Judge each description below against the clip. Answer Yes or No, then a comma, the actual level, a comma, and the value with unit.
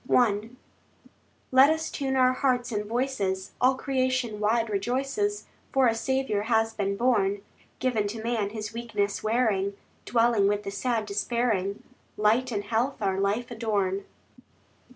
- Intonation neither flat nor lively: Yes, average, 3.7 semitones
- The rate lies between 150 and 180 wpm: No, average, 140 wpm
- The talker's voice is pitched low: No, high, 225 Hz